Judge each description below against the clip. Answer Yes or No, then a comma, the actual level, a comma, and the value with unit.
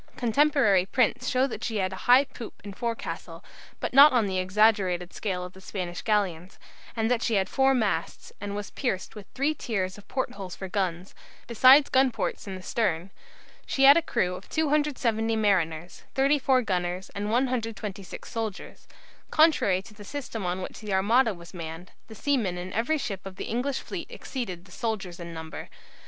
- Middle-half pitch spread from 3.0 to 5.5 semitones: Yes, average, 5.1 semitones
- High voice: Yes, high, 210 Hz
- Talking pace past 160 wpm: Yes, average, 185 wpm